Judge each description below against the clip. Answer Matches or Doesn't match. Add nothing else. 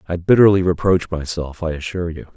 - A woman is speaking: Doesn't match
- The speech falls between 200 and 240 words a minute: Doesn't match